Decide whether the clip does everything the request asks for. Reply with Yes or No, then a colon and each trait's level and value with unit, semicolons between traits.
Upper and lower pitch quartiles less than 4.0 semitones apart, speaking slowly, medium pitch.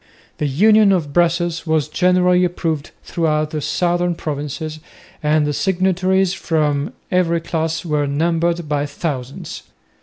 Yes: average, 2.9 semitones; slow, 125 wpm; medium, 165 Hz